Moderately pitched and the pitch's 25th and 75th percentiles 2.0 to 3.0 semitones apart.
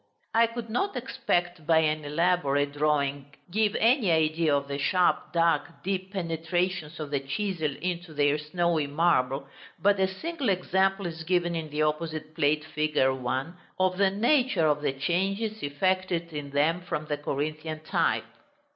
No: medium, 165 Hz; average, 4.0 semitones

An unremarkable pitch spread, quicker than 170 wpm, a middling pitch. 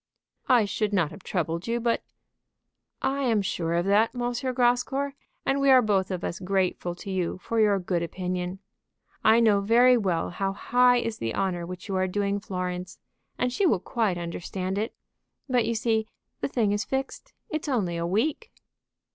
No: average, 4.8 semitones; average, 185 wpm; high, 205 Hz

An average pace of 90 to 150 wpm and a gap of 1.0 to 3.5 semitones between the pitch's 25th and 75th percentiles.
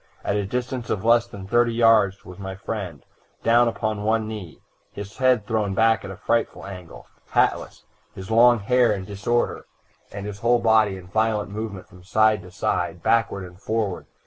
No: average, 180 wpm; average, 2.8 semitones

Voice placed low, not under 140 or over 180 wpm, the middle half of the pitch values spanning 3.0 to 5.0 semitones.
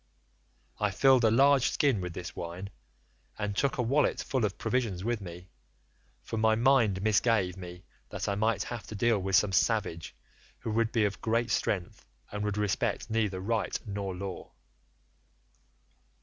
Yes: low, 105 Hz; average, 165 wpm; average, 3.3 semitones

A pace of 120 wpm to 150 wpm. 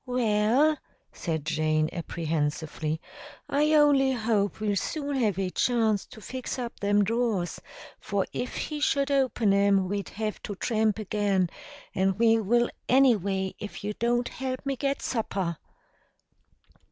Yes: average, 140 wpm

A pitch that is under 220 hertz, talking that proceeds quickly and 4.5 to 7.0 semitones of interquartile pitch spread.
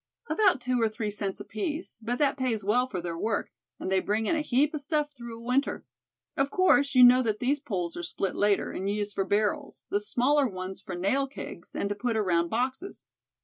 No: high, 230 Hz; fast, 220 wpm; average, 5.2 semitones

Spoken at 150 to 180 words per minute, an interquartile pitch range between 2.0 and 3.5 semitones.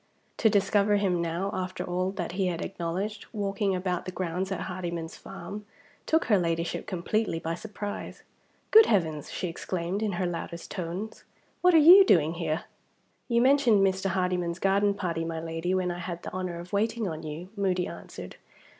Yes: average, 175 wpm; average, 3.0 semitones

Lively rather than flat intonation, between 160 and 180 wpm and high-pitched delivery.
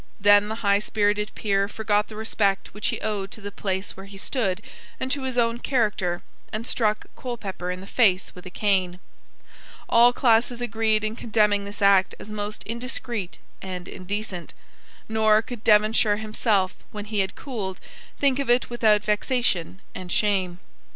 No: narrow, 2.5 semitones; average, 165 wpm; high, 210 Hz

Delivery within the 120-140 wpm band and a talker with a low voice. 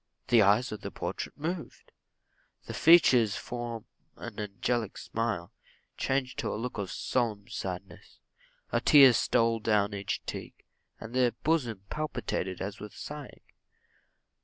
Yes: slow, 135 wpm; low, 115 Hz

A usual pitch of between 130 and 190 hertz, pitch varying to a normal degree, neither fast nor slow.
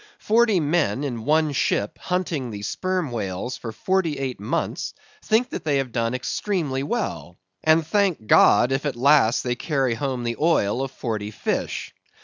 No: low, 135 Hz; wide, 5.7 semitones; average, 160 wpm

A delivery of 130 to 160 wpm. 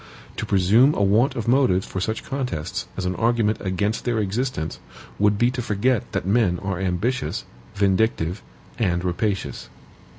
Yes: average, 155 wpm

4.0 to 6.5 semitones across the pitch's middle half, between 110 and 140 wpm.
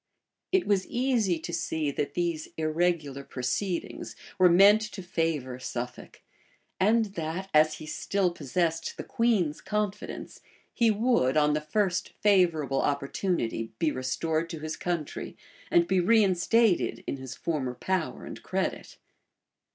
Yes: average, 4.5 semitones; slow, 135 wpm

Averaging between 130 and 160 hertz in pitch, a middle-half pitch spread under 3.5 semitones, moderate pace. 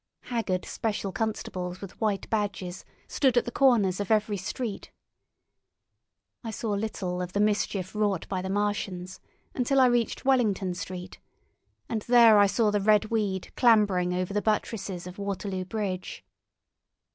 No: high, 205 Hz; average, 3.0 semitones; average, 145 wpm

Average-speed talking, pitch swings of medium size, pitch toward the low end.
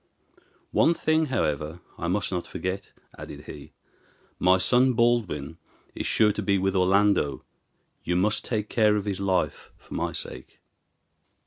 Yes: average, 145 wpm; average, 3.2 semitones; low, 100 Hz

